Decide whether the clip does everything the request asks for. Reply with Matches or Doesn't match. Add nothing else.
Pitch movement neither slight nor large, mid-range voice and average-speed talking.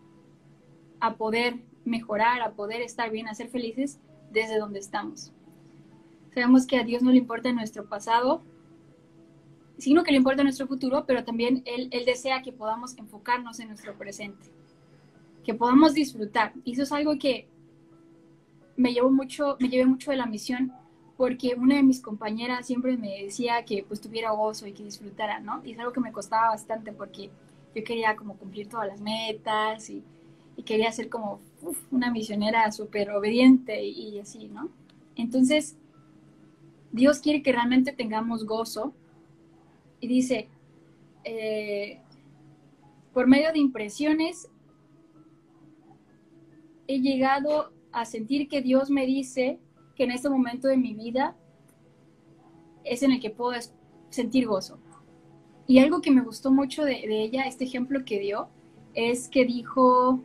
Doesn't match